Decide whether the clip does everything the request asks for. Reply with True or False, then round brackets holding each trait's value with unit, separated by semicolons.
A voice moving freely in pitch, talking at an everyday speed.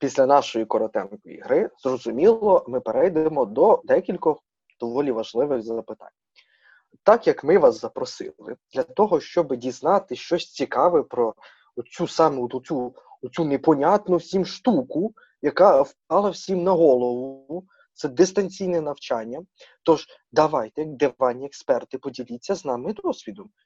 True (6.9 semitones; 115 wpm)